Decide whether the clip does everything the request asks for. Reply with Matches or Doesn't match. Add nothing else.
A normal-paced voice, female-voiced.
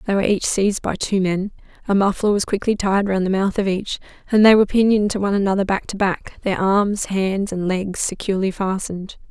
Doesn't match